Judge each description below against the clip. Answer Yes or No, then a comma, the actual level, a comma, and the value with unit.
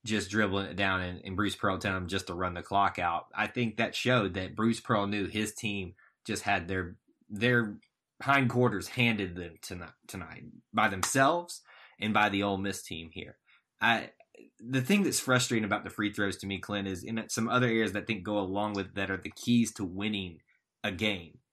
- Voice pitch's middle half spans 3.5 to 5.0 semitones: No, average, 2.8 semitones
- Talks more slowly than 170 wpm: No, fast, 205 wpm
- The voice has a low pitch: Yes, low, 105 Hz